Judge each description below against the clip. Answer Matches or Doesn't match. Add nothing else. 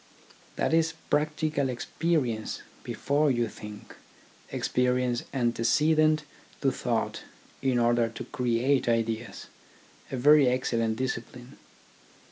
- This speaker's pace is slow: Matches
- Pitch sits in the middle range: Doesn't match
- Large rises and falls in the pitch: Doesn't match